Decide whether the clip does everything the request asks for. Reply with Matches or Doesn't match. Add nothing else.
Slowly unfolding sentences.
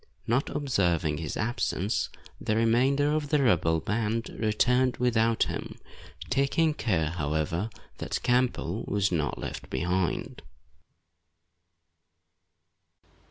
Matches